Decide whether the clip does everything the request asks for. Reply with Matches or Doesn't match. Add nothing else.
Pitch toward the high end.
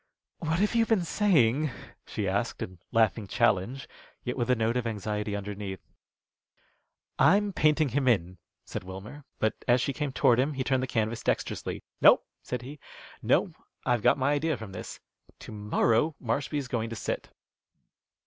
Doesn't match